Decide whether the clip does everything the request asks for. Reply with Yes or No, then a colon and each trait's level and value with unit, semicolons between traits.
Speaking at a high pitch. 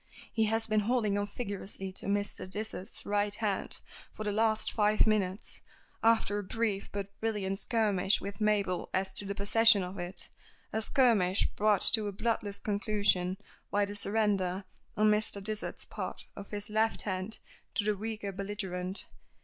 Yes: high, 205 Hz